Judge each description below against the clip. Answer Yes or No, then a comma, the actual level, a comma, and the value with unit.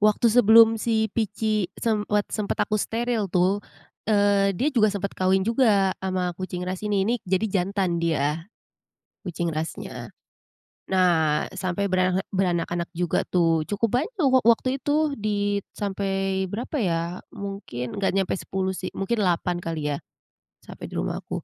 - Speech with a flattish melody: No, average, 3.0 semitones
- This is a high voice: Yes, high, 195 Hz